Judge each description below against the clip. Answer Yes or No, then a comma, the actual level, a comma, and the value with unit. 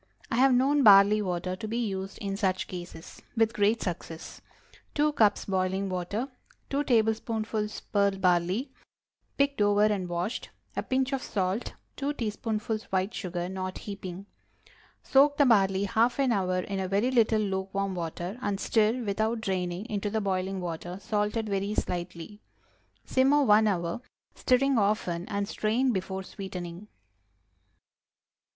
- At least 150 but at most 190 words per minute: No, average, 140 wpm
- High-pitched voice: Yes, high, 205 Hz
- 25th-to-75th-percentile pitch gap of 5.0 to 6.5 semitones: No, average, 3.2 semitones